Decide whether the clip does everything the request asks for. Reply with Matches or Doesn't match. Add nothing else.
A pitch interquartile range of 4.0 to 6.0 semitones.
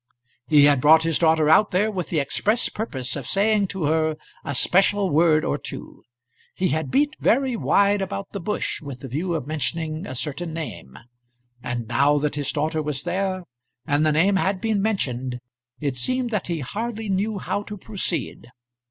Matches